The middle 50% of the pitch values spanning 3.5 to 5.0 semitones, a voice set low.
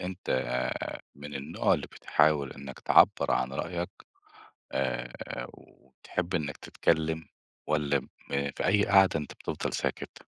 Yes: average, 4.1 semitones; very low, 75 Hz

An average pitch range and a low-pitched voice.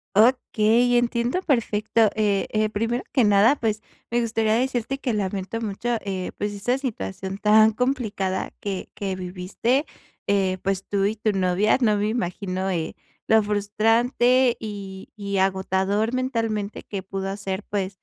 No: average, 3.2 semitones; high, 210 Hz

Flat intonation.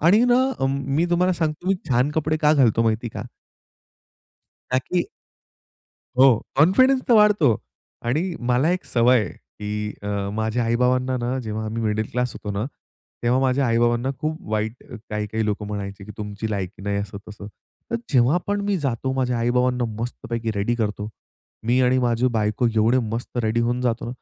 No: average, 3.8 semitones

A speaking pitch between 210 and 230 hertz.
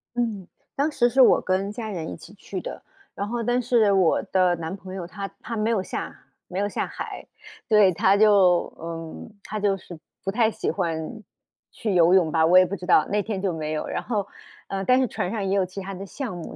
No: high, 195 Hz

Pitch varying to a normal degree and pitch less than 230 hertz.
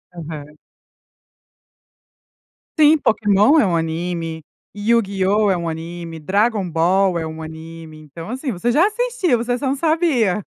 No: wide, 6.7 semitones; high, 190 Hz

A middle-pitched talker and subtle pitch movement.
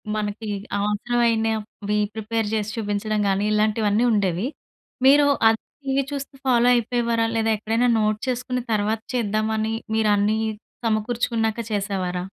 No: high, 220 Hz; narrow, 2.0 semitones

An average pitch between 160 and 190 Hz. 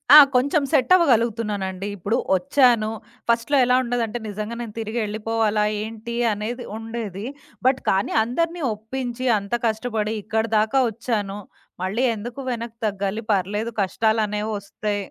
No: high, 220 Hz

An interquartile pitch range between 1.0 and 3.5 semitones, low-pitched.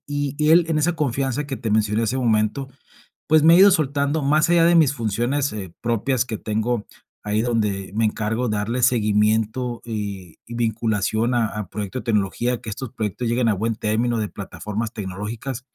No: average, 4.0 semitones; low, 115 Hz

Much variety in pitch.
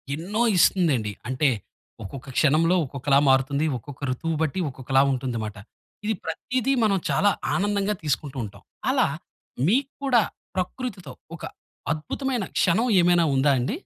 Yes: wide, 7.1 semitones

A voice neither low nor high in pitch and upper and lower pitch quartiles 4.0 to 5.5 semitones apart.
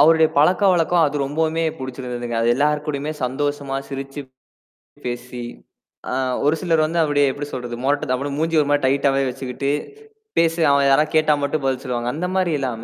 No: medium, 145 Hz; average, 3.1 semitones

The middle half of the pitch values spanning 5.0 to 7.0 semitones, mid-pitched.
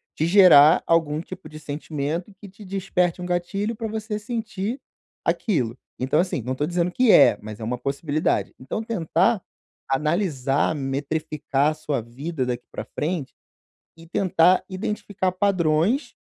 Yes: average, 5.3 semitones; medium, 165 Hz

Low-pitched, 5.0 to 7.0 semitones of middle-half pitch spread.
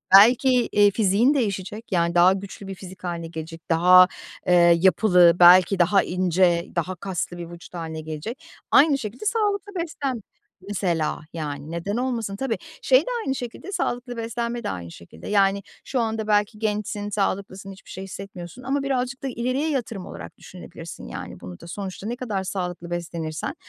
No: high, 195 Hz; average, 5.3 semitones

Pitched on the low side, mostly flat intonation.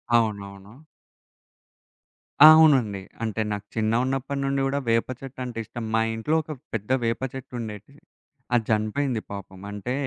No: low, 115 Hz; average, 4.1 semitones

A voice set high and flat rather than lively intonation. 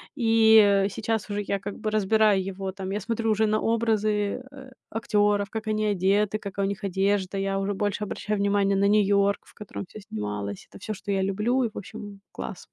Yes: high, 205 Hz; narrow, 1.6 semitones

